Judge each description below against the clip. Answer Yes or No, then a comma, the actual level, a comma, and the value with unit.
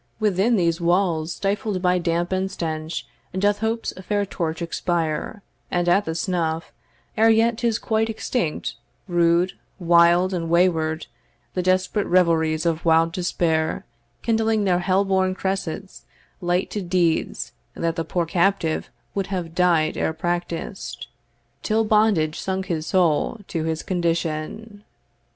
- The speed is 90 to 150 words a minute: Yes, slow, 135 wpm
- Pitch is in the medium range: Yes, medium, 180 Hz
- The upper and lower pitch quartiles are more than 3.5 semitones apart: No, average, 2.9 semitones